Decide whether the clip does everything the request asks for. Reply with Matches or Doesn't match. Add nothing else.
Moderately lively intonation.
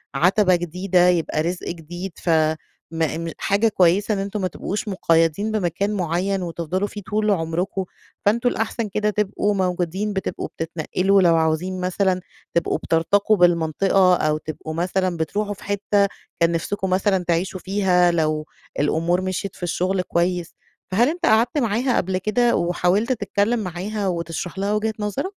Matches